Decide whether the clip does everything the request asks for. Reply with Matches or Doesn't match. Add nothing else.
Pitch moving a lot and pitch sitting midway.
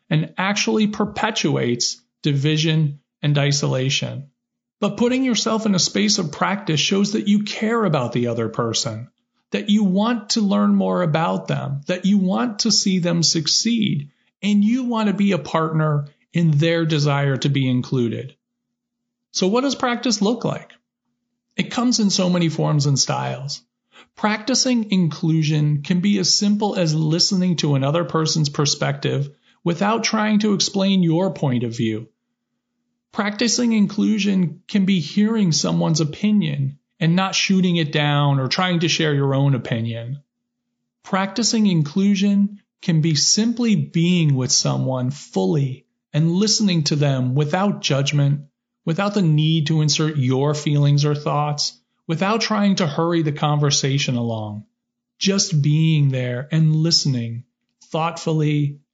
Matches